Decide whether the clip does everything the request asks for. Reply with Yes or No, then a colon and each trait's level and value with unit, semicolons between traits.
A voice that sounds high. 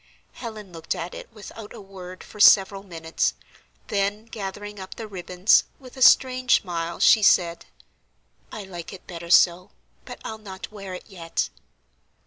Yes: high, 195 Hz